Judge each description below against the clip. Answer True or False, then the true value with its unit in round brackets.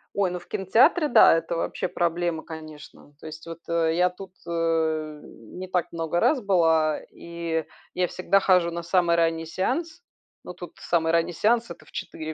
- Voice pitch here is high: False (170 Hz)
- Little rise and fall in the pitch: True (2.1 semitones)